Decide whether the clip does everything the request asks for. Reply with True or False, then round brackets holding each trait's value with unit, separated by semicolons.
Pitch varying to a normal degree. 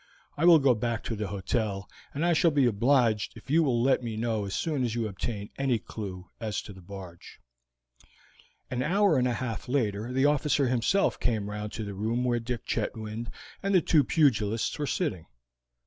True (4.6 semitones)